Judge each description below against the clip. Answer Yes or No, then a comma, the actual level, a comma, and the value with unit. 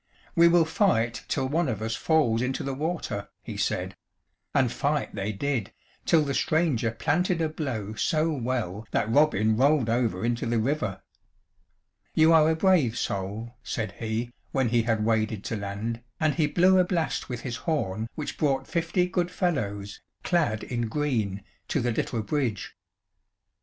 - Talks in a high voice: No, low, 125 Hz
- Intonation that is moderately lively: No, wide, 6.0 semitones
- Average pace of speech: Yes, average, 165 wpm